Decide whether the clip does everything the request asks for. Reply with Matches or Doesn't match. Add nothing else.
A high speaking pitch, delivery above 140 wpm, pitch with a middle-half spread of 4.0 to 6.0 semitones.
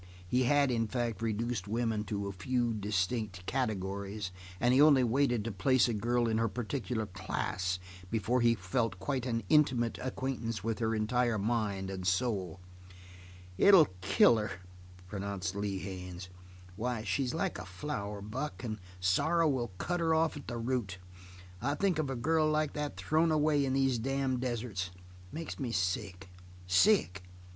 Doesn't match